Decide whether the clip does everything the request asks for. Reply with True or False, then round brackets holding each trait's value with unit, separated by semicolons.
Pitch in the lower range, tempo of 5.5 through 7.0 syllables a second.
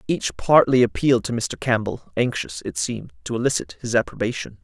True (115 Hz; 5.6 syllables/s)